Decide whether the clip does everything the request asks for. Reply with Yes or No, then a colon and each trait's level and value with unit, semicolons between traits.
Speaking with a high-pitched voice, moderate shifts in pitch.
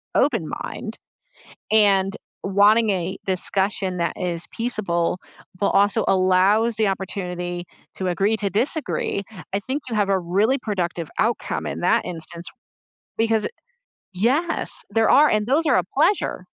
Yes: high, 200 Hz; average, 3.4 semitones